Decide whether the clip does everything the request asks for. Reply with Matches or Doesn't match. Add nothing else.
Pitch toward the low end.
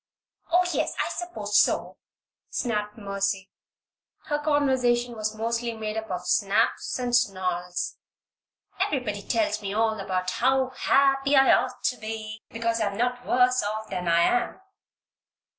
Doesn't match